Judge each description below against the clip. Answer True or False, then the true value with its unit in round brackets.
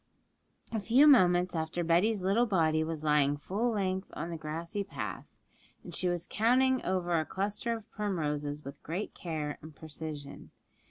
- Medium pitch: True (175 Hz)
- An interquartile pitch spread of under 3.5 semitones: False (4.7 semitones)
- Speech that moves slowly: False (160 wpm)